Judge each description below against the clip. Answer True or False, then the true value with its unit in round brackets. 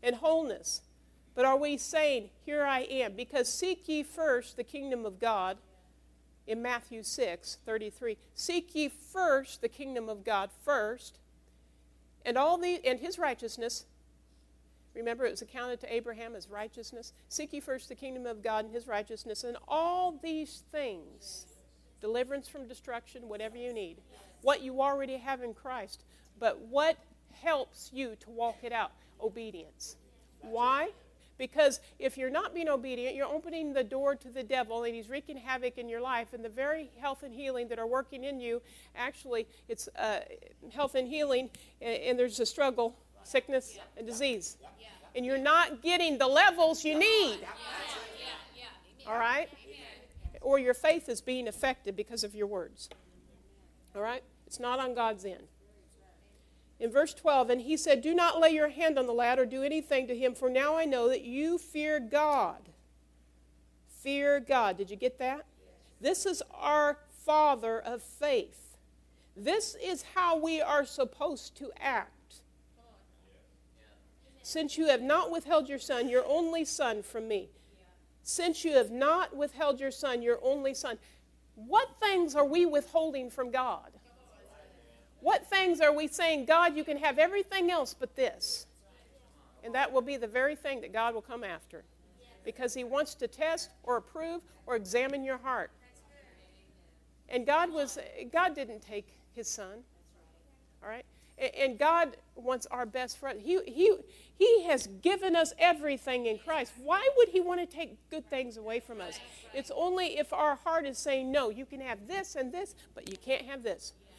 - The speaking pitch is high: True (265 Hz)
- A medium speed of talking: True (165 wpm)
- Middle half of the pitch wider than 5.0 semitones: False (4.7 semitones)